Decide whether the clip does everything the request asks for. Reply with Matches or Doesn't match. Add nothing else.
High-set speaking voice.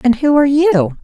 Matches